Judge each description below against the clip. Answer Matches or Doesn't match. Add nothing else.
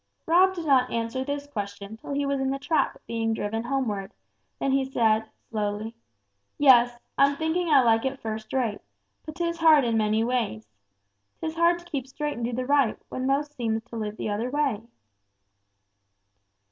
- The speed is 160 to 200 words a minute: Matches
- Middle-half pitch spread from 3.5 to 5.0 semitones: Matches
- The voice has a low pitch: Doesn't match